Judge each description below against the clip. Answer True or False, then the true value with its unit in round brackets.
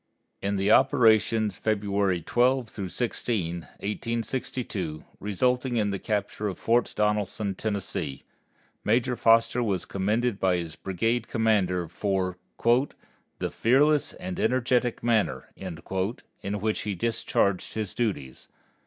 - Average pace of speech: False (110 wpm)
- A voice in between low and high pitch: False (105 Hz)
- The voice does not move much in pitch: False (3.7 semitones)